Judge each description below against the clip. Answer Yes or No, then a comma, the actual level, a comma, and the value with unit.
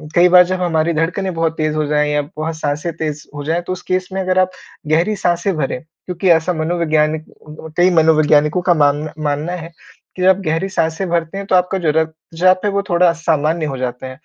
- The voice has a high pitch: No, medium, 165 Hz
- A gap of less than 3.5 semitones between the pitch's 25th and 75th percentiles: Yes, average, 2.7 semitones